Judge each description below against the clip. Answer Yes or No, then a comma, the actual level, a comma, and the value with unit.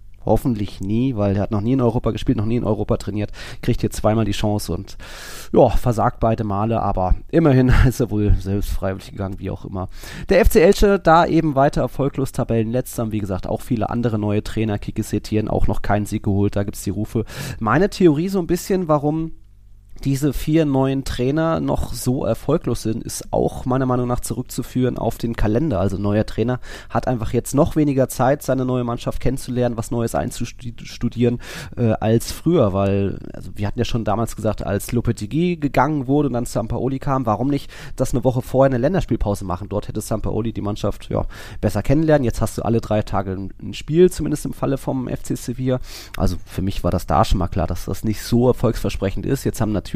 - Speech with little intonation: No, average, 4.2 semitones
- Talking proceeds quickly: Yes, fast, 205 wpm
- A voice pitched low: Yes, low, 115 Hz